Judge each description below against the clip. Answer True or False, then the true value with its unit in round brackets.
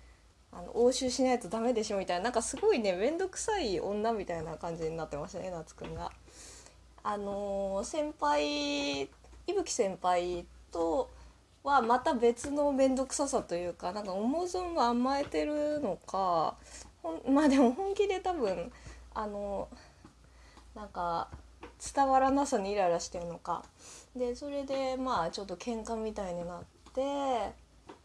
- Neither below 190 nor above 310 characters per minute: True (280 characters per minute)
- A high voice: True (230 Hz)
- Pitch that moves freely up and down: True (8.0 semitones)